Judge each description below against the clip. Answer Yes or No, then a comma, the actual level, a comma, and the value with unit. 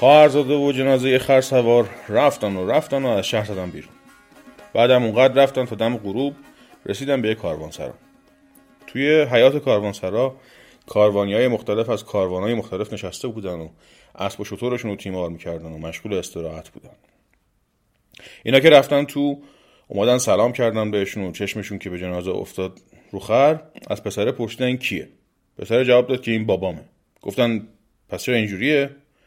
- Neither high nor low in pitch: No, low, 120 Hz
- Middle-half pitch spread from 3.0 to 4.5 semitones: No, average, 5.1 semitones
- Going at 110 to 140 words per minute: No, fast, 155 wpm